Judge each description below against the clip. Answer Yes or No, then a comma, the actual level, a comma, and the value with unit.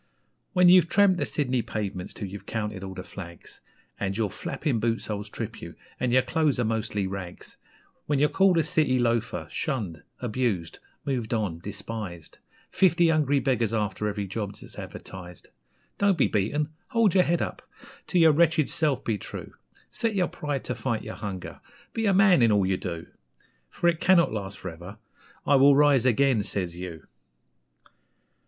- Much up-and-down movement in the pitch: Yes, wide, 7.4 semitones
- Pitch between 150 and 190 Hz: No, low, 115 Hz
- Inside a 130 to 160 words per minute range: No, average, 175 wpm